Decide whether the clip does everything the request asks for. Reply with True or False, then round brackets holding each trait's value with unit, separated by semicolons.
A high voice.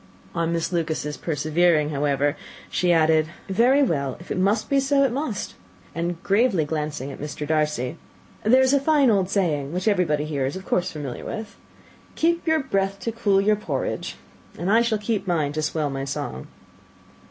False (175 Hz)